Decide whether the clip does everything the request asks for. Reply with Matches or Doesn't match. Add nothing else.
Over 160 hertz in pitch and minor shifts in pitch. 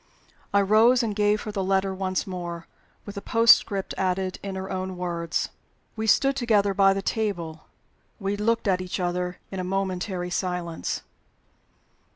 Matches